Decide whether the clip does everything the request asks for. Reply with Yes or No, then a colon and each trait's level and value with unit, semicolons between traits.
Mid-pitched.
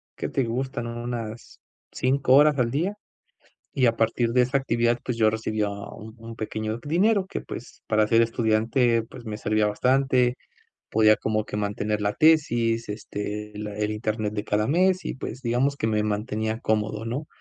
No: low, 115 Hz